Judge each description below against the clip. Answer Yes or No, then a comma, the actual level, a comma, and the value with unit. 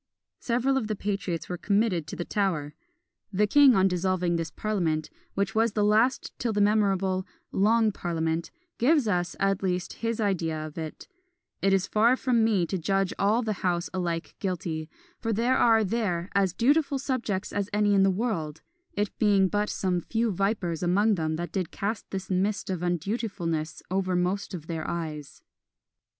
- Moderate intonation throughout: Yes, average, 3.7 semitones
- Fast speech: No, average, 175 wpm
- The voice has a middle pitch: No, high, 195 Hz